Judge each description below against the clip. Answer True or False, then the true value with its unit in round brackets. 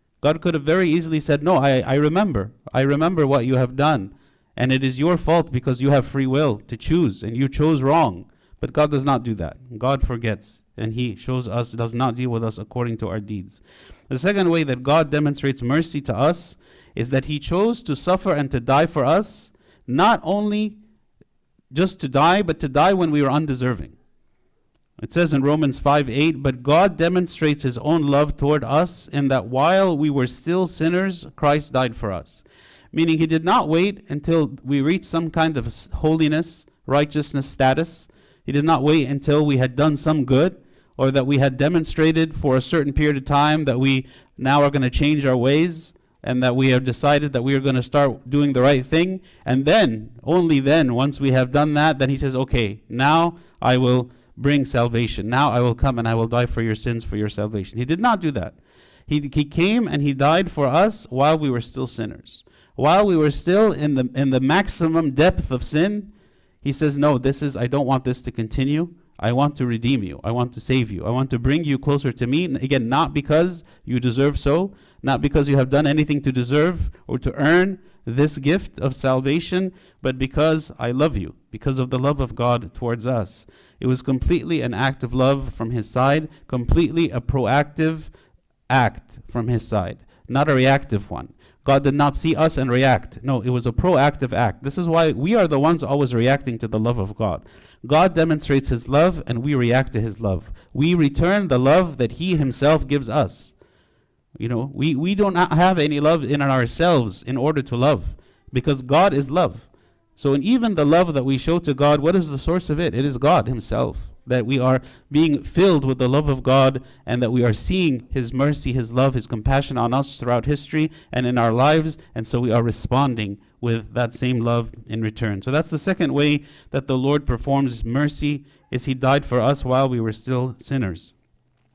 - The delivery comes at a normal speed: False (210 wpm)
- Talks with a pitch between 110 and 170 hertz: True (140 Hz)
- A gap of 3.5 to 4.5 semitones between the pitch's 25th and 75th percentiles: True (3.8 semitones)